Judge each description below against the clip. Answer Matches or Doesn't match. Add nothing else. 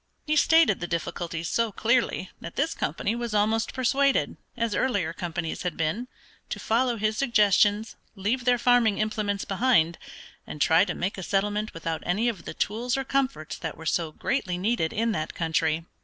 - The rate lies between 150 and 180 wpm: Matches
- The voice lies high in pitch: Matches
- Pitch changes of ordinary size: Doesn't match